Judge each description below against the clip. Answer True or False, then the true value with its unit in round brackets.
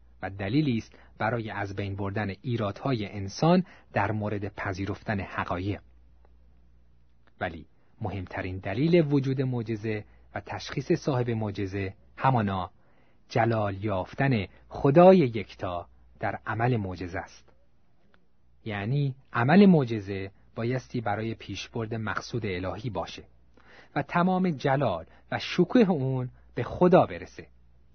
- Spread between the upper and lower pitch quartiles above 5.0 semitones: True (5.5 semitones)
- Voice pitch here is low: True (105 Hz)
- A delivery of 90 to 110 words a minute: True (105 wpm)